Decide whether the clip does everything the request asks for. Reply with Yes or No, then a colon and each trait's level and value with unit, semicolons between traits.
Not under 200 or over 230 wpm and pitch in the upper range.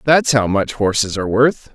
No: fast, 205 wpm; low, 120 Hz